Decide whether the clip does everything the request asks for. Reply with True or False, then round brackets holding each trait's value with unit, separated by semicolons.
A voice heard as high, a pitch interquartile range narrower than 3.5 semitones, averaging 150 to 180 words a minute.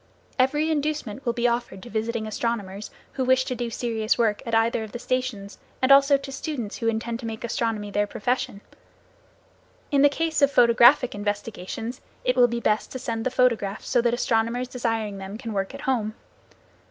False (235 Hz; 2.8 semitones; 190 wpm)